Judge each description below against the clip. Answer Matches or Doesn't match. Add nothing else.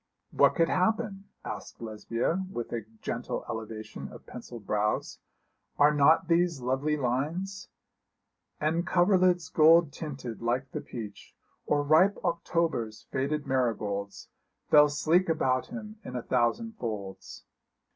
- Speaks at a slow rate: Matches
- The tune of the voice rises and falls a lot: Matches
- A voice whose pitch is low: Doesn't match